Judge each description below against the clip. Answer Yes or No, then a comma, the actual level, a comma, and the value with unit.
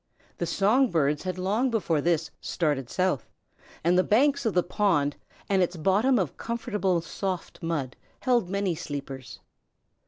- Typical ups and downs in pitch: Yes, average, 4.4 semitones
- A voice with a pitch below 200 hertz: Yes, medium, 185 Hz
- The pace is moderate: Yes, average, 150 wpm